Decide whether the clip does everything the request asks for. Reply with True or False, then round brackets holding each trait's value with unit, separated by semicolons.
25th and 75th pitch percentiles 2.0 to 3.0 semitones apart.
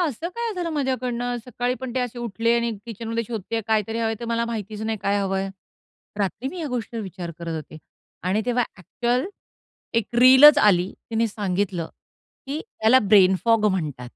False (3.7 semitones)